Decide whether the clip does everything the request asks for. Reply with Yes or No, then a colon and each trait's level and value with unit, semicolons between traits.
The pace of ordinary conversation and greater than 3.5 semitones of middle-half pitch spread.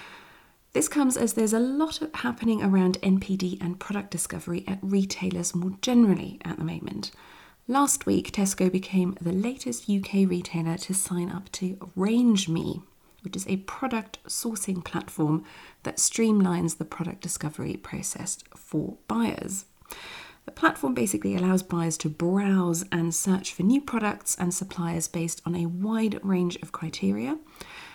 Yes: average, 145 wpm; average, 4.1 semitones